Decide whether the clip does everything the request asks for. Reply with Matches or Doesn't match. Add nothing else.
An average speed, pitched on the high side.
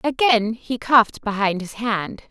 Matches